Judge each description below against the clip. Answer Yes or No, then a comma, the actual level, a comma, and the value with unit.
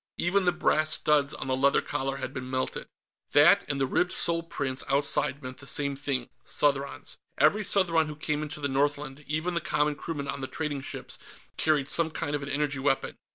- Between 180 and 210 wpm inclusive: Yes, average, 200 wpm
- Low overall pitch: No, medium, 145 Hz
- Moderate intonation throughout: No, narrow, 2.2 semitones